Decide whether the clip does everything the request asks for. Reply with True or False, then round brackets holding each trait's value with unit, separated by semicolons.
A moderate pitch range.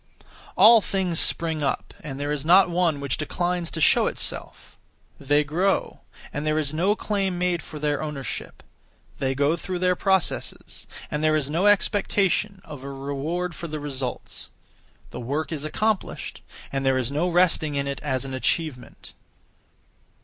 True (4.2 semitones)